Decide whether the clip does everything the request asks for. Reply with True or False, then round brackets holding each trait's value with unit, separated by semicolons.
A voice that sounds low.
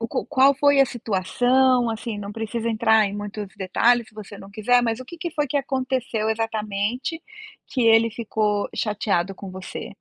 False (225 Hz)